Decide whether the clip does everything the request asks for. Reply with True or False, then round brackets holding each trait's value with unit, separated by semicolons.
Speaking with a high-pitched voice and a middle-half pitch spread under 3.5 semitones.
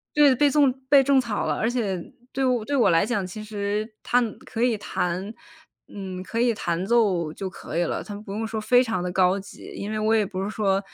False (215 Hz; 3.8 semitones)